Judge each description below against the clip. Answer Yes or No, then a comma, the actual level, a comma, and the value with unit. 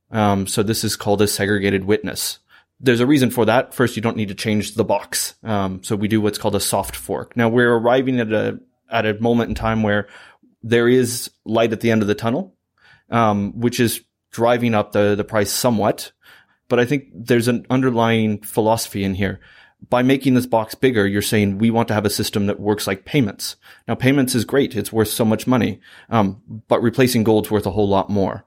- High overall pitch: No, low, 110 Hz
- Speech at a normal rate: No, fast, 235 wpm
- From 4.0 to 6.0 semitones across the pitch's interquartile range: No, narrow, 2.4 semitones